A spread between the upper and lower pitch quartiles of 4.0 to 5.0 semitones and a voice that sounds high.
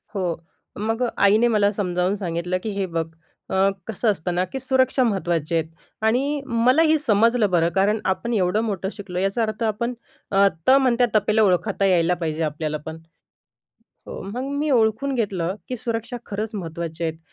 Yes: average, 4.6 semitones; high, 205 Hz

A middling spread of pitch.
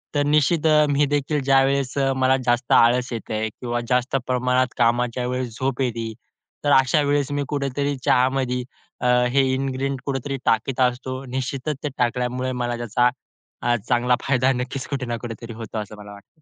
No: narrow, 2.2 semitones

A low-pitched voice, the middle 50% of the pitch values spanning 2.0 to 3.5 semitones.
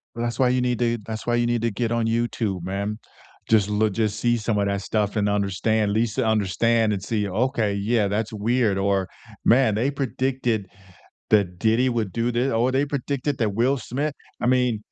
Yes: low, 115 Hz; average, 2.9 semitones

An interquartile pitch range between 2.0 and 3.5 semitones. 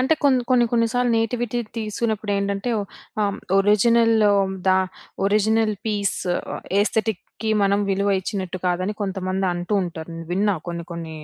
Yes: average, 2.9 semitones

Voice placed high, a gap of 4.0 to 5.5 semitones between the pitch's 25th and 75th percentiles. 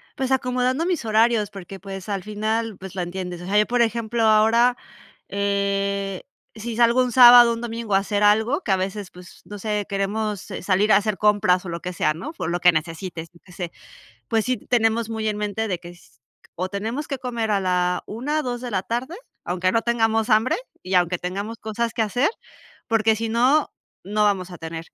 No: high, 210 Hz; average, 3.6 semitones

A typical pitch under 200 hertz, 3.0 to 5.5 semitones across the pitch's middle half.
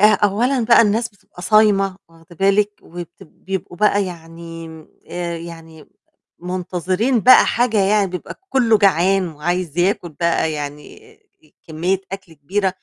Yes: medium, 185 Hz; average, 3.7 semitones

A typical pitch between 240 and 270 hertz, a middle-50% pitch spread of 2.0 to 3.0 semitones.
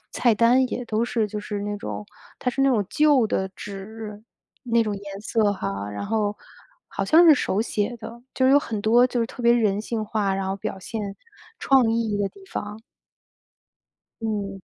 No: high, 220 Hz; narrow, 2.6 semitones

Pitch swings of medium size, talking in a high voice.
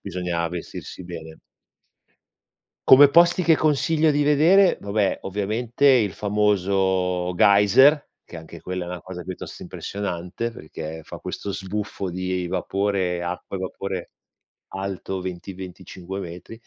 No: average, 3.2 semitones; very low, 95 Hz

